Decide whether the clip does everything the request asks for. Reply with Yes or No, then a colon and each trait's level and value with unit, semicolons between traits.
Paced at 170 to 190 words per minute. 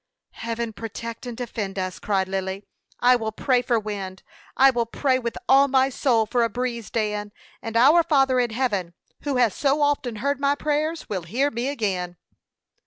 Yes: average, 180 wpm